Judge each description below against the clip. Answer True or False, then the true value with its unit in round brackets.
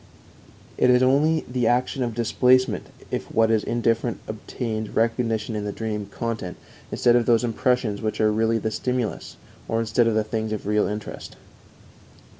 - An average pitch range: False (2.2 semitones)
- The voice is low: True (115 Hz)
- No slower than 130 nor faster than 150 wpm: False (165 wpm)